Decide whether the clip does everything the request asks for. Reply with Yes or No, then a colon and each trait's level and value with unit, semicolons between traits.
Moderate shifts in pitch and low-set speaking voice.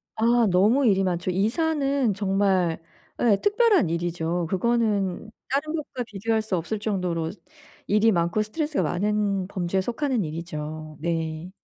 No: average, 5.0 semitones; high, 200 Hz